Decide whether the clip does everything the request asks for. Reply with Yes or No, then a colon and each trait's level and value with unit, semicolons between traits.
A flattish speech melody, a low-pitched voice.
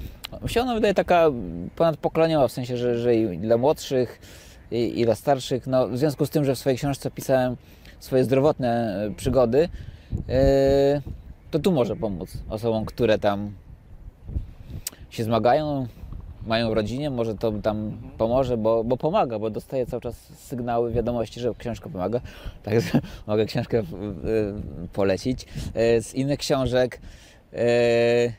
No: average, 3.6 semitones; low, 120 Hz